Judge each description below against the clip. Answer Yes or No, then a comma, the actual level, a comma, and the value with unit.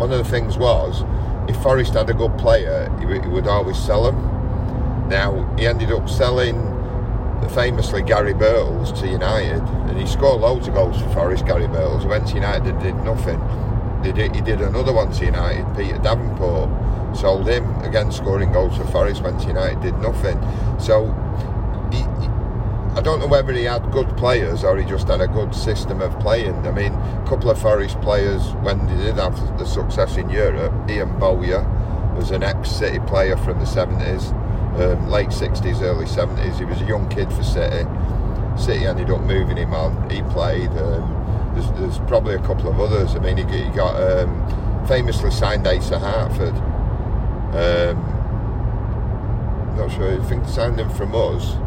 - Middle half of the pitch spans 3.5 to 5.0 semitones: No, narrow, 2.4 semitones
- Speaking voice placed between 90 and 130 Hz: Yes, low, 105 Hz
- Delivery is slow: No, average, 180 wpm